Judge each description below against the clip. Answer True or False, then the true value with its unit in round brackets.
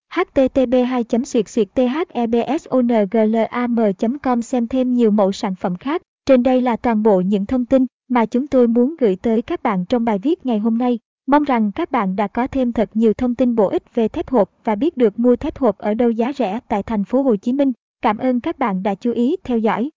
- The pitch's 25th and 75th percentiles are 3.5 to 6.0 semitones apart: False (2.7 semitones)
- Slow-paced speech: False (215 wpm)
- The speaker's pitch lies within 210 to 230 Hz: False (240 Hz)